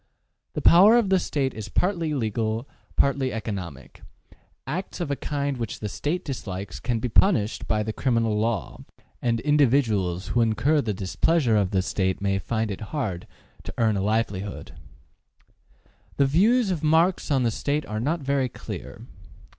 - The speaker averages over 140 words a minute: Yes, average, 160 wpm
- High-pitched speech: No, low, 120 Hz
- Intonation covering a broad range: Yes, wide, 5.7 semitones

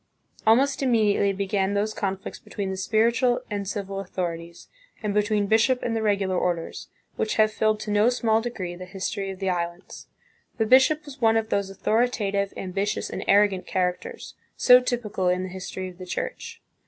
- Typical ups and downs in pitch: Yes, average, 3.0 semitones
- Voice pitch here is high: Yes, high, 205 Hz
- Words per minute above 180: No, average, 175 wpm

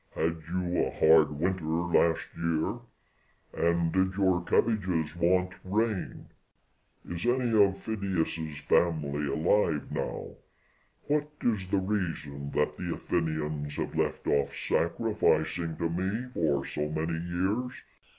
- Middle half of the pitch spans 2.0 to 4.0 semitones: Yes, average, 3.4 semitones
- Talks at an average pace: No, slow, 120 wpm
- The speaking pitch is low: Yes, very low, 85 Hz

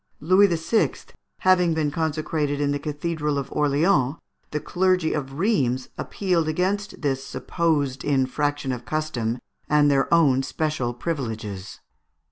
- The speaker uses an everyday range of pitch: Yes, average, 3.6 semitones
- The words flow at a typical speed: No, slow, 125 wpm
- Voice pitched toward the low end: No, medium, 150 Hz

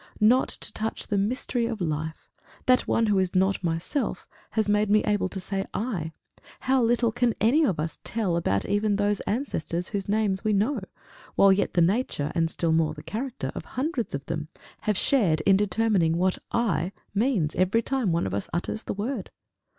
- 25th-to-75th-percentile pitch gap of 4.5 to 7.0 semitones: Yes, average, 5.0 semitones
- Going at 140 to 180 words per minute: No, average, 190 wpm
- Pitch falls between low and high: No, high, 205 Hz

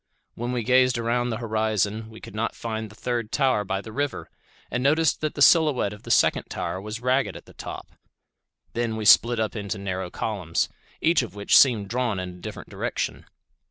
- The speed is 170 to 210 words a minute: Yes, average, 200 wpm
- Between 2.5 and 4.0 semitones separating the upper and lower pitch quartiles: Yes, average, 3.3 semitones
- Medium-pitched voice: No, low, 115 Hz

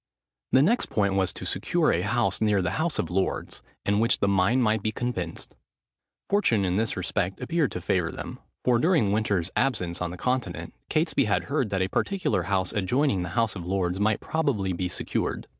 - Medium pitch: No, low, 100 Hz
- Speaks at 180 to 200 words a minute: Yes, average, 195 wpm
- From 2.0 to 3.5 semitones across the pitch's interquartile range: No, average, 5.1 semitones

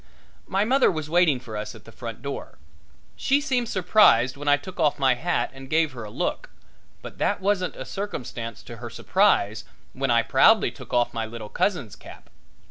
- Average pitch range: No, wide, 8.0 semitones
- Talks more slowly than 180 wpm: No, average, 195 wpm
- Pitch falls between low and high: Yes, medium, 145 Hz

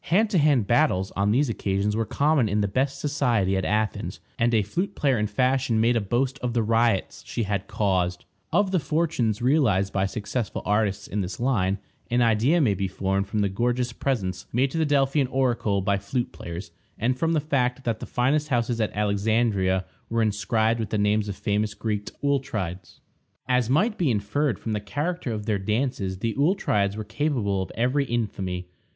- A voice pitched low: Yes, low, 115 Hz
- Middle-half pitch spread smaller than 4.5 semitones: No, average, 4.8 semitones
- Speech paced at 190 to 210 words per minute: Yes, average, 195 wpm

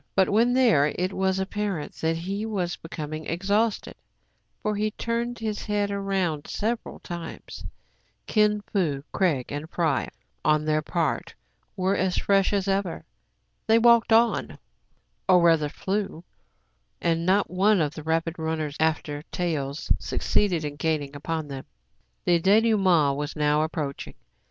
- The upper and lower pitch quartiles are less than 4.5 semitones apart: No, average, 4.8 semitones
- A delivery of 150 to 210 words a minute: No, average, 140 wpm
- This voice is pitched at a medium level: Yes, medium, 175 Hz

